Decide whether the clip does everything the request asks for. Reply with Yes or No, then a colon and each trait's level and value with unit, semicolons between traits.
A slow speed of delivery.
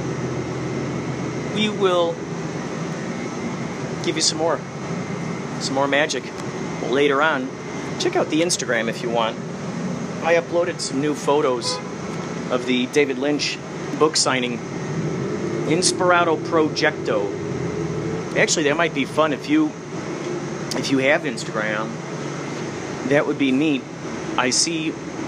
Yes: slow, 115 wpm